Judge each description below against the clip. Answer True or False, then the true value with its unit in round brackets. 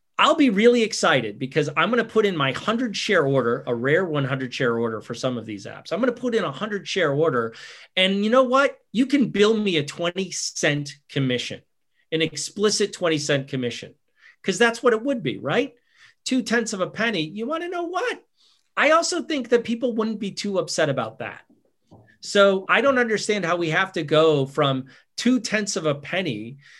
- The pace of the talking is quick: True (210 wpm)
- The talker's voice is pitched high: True (195 Hz)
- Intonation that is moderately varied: False (7.9 semitones)